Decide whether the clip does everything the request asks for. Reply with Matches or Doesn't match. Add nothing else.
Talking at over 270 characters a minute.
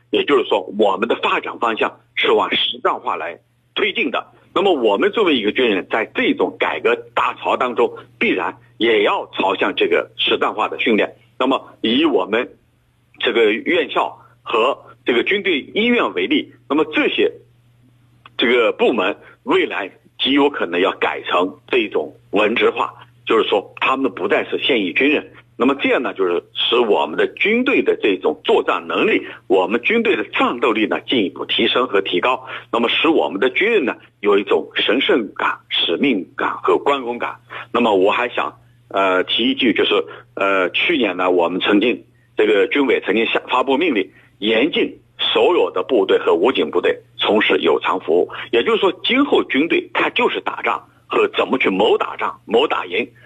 Doesn't match